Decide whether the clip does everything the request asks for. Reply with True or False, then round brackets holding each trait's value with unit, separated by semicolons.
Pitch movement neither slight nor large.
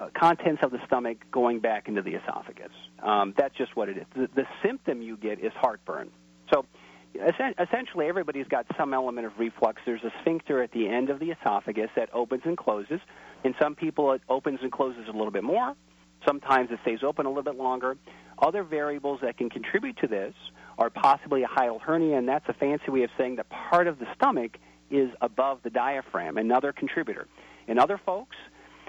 True (4.7 semitones)